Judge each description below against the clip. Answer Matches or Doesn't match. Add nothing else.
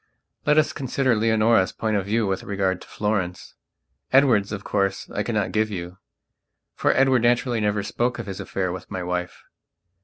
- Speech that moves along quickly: Doesn't match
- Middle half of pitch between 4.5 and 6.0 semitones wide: Doesn't match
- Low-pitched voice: Matches